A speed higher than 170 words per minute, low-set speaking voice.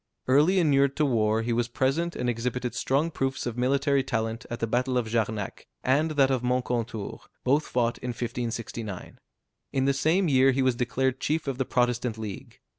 Yes: average, 185 wpm; low, 125 Hz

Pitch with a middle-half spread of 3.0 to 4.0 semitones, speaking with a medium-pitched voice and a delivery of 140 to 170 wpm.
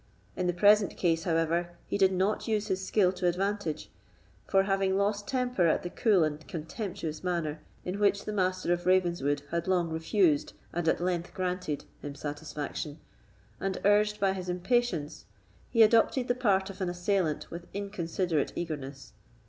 Yes: average, 3.4 semitones; medium, 180 Hz; average, 165 wpm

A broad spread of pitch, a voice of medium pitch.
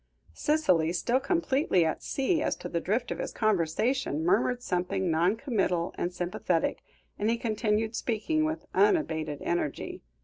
No: wide, 7.0 semitones; high, 215 Hz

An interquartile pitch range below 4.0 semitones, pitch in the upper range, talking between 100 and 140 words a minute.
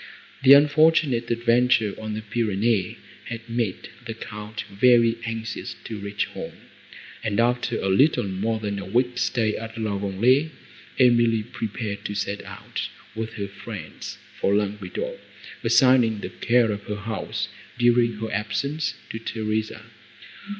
No: narrow, 2.5 semitones; low, 110 Hz; slow, 135 wpm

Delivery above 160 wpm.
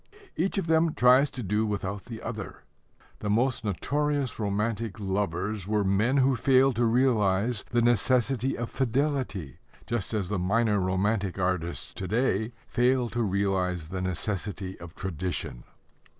No: average, 145 wpm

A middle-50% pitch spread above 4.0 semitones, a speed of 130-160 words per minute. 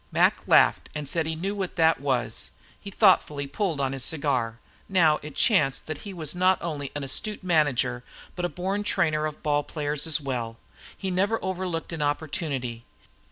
No: average, 4.5 semitones; average, 180 wpm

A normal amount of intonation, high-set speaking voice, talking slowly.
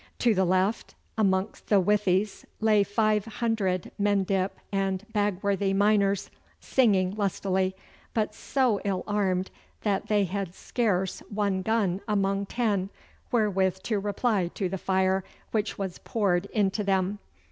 No: narrow, 1.8 semitones; high, 200 Hz; slow, 130 wpm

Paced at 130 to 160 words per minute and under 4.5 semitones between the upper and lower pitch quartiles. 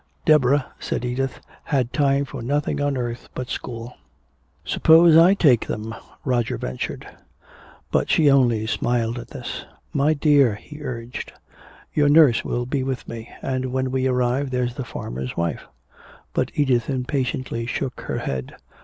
Yes: average, 150 wpm; average, 2.9 semitones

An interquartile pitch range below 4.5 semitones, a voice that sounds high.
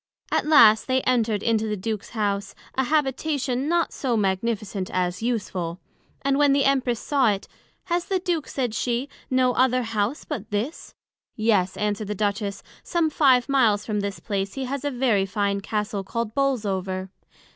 No: average, 4.8 semitones; high, 230 Hz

